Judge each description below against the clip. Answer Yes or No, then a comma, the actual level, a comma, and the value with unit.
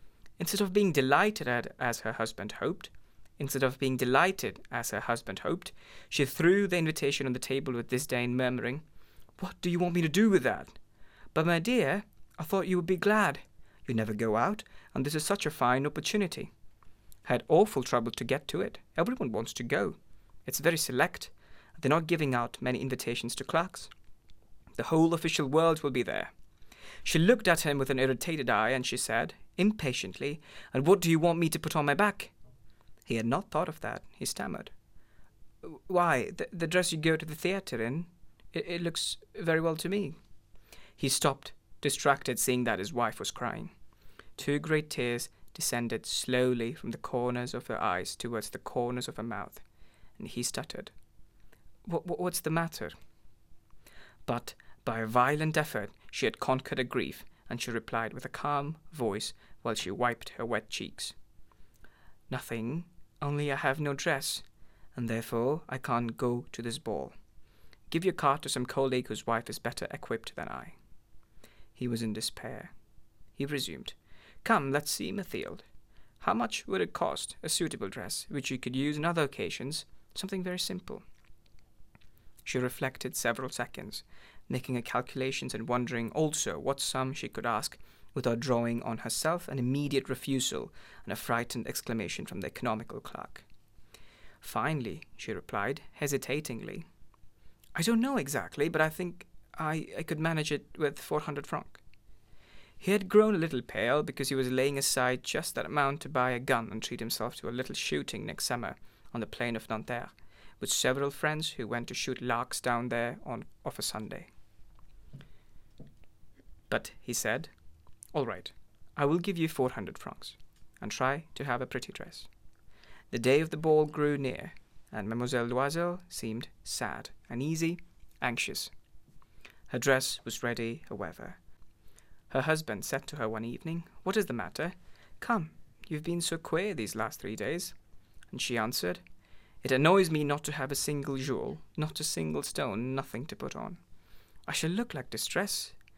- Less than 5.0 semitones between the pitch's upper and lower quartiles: No, average, 5.3 semitones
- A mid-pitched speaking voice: No, low, 130 Hz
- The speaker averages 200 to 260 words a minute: No, average, 175 wpm